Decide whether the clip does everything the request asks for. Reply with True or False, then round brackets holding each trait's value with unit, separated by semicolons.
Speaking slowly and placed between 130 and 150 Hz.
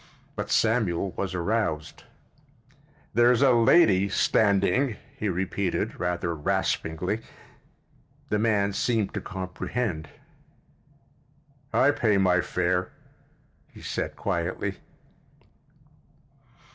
False (85 wpm; 100 Hz)